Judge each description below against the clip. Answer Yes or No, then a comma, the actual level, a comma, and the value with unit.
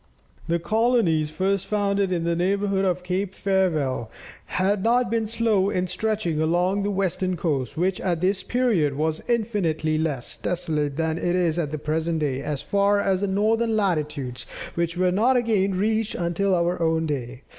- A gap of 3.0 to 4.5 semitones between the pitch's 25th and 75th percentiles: Yes, average, 4.0 semitones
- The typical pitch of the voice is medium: Yes, medium, 180 Hz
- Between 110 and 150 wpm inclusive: No, average, 165 wpm